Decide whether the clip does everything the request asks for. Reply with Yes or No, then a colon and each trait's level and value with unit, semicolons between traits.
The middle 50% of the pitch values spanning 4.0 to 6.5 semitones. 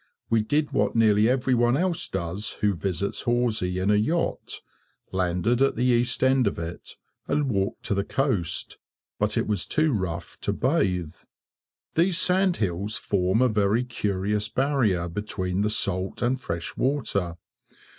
Yes: average, 5.3 semitones